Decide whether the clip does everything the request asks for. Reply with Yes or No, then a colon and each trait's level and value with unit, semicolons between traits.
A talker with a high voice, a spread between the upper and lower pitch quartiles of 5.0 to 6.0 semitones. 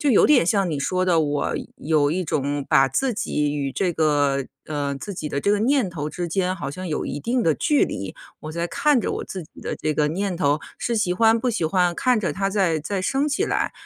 No: medium, 175 Hz; wide, 5.5 semitones